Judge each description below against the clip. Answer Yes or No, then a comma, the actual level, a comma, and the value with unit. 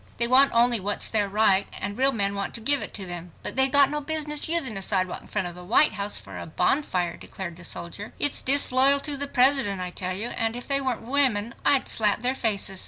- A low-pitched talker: No, high, 225 Hz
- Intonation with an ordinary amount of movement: No, wide, 5.7 semitones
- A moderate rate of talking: No, fast, 240 wpm